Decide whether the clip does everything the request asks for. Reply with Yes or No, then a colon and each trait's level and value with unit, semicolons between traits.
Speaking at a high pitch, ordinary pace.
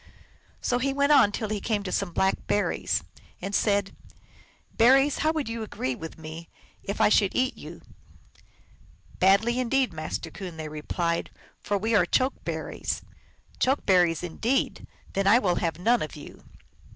Yes: high, 200 Hz; average, 175 wpm